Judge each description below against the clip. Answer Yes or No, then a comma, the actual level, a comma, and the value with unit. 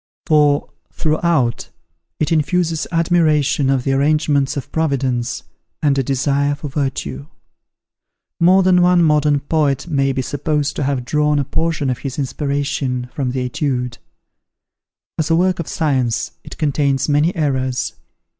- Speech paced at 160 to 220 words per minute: No, average, 140 wpm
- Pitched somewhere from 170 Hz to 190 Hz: No, medium, 145 Hz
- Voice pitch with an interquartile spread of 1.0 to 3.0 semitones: Yes, average, 2.7 semitones